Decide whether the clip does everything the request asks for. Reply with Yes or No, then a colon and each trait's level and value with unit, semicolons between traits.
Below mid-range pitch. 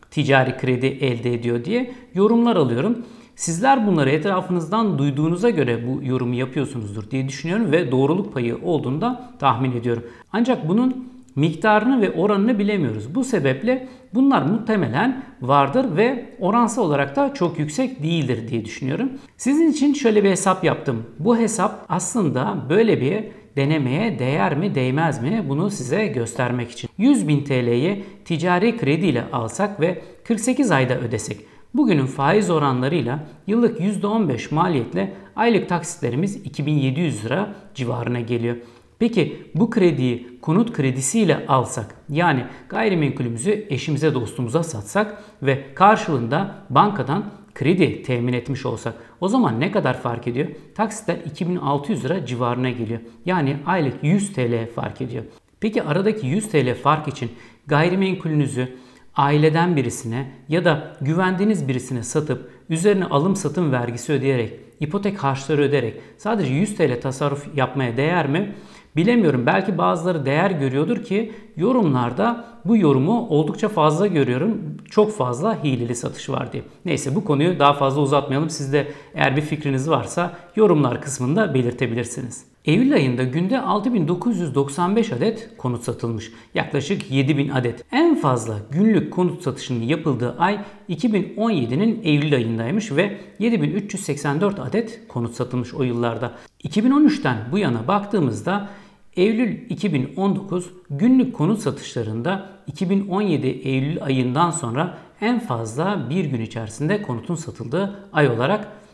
No: medium, 155 Hz